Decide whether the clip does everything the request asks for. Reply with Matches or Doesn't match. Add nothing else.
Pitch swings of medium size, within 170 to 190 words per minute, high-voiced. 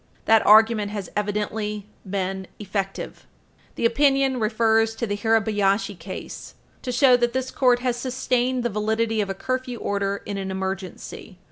Doesn't match